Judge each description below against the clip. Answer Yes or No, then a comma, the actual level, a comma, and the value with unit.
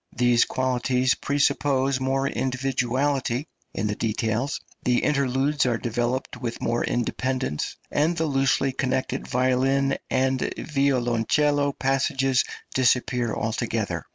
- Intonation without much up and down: Yes, narrow, 1.9 semitones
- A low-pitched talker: Yes, low, 130 Hz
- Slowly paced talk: Yes, slow, 105 wpm